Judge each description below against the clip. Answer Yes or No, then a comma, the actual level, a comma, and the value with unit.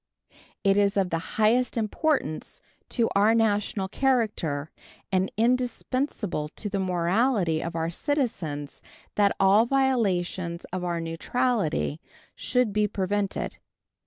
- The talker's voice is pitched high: Yes, high, 200 Hz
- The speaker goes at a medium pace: No, slow, 115 wpm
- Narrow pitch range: No, average, 5.3 semitones